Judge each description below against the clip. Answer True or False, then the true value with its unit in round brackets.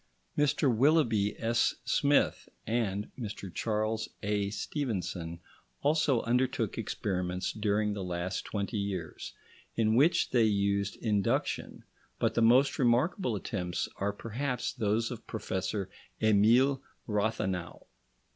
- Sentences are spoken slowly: True (110 wpm)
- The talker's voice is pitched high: False (110 Hz)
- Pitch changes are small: False (3.5 semitones)